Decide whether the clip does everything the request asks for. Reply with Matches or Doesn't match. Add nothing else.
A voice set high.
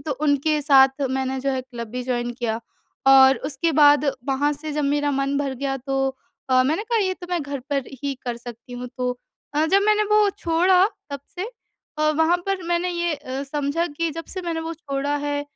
Matches